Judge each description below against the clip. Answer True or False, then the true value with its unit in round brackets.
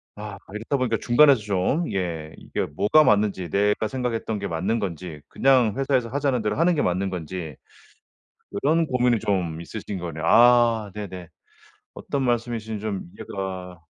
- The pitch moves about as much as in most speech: True (4.9 semitones)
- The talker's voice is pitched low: True (105 Hz)